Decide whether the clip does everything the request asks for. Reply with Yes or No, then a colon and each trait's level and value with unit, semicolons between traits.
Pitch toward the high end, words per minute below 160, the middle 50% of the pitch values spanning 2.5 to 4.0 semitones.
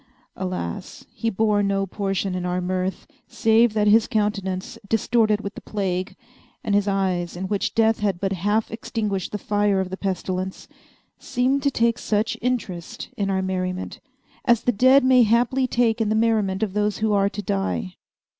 No: high, 205 Hz; average, 175 wpm; average, 3.0 semitones